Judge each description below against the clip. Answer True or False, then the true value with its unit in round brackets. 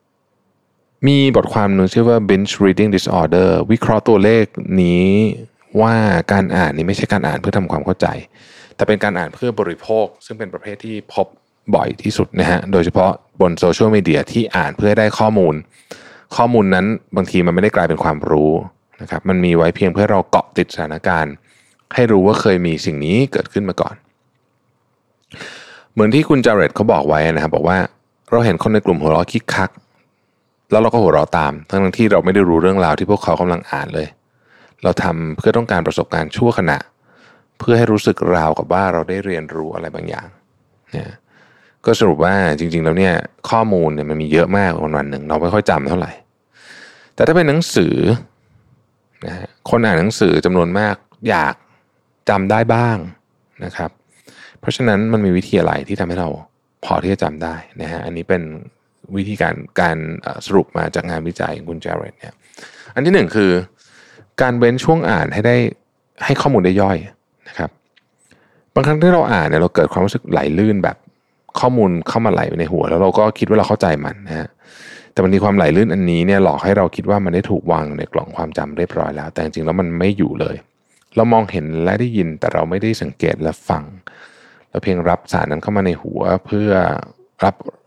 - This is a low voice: True (95 Hz)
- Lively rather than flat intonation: False (4.3 semitones)